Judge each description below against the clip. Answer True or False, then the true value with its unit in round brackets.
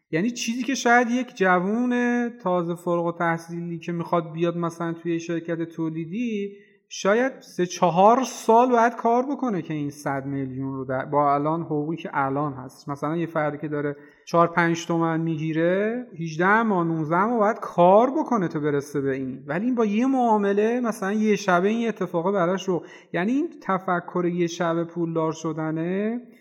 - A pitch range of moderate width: True (5.0 semitones)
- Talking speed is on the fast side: True (170 wpm)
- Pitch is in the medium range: True (175 Hz)